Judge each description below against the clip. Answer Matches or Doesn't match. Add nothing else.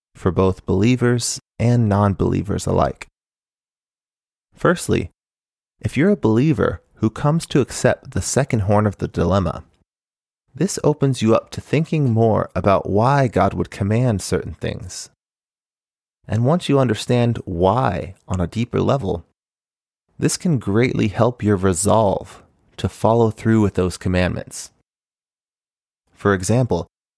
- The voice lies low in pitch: Matches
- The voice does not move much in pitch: Doesn't match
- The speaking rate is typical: Doesn't match